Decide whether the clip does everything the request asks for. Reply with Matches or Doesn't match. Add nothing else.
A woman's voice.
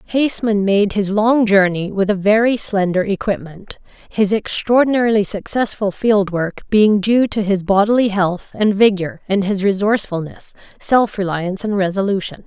Matches